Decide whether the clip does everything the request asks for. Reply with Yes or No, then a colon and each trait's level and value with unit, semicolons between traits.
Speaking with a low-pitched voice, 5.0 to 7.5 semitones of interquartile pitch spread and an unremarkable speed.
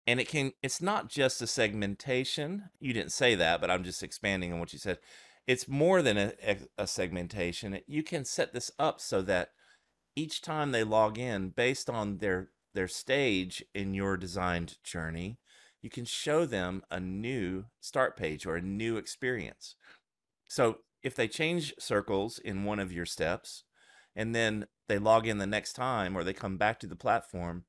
Yes: low, 105 Hz; wide, 5.6 semitones; average, 180 wpm